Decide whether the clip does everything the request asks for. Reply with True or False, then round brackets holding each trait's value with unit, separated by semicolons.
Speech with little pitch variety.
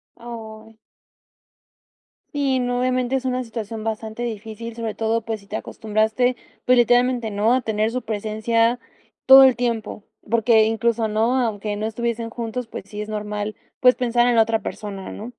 True (2.1 semitones)